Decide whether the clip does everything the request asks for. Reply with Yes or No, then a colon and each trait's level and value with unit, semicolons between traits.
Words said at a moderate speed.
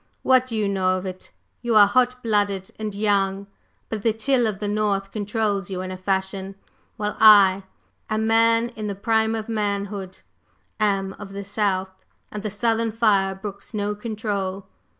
Yes: average, 170 wpm